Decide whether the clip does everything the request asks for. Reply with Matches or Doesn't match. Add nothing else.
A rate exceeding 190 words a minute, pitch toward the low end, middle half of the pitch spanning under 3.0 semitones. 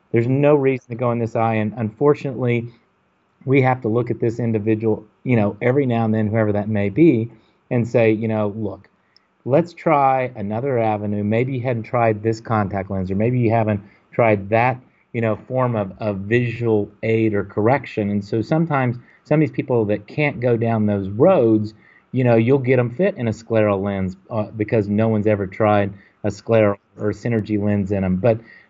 Matches